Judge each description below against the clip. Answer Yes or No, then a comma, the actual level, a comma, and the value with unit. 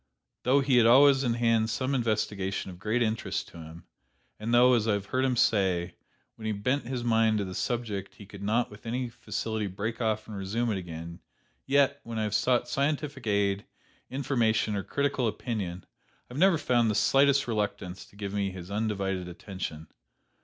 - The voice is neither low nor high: No, low, 110 Hz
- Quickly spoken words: No, average, 190 wpm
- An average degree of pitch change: Yes, average, 3.7 semitones